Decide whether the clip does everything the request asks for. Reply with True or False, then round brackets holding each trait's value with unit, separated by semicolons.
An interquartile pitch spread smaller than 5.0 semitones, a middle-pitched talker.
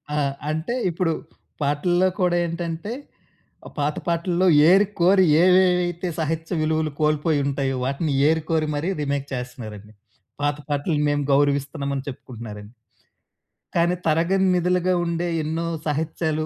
True (3.5 semitones; 160 Hz)